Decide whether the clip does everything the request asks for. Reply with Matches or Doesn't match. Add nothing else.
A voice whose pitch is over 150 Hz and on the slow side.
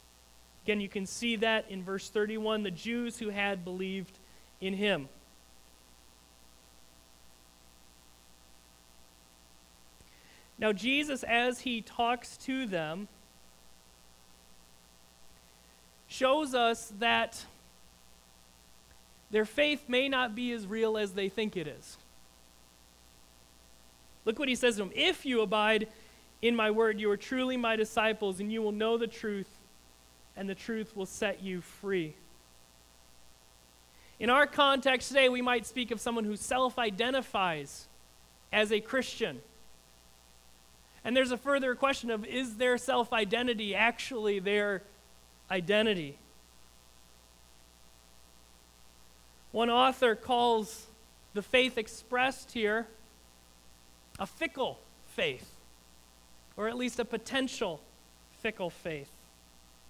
Matches